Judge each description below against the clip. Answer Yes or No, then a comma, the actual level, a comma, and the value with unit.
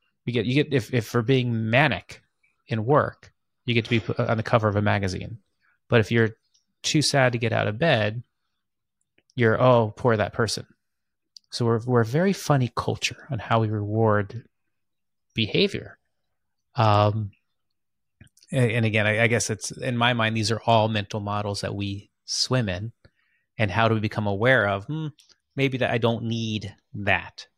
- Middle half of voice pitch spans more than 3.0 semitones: No, narrow, 2.6 semitones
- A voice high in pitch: No, low, 115 Hz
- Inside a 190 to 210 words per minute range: No, average, 180 wpm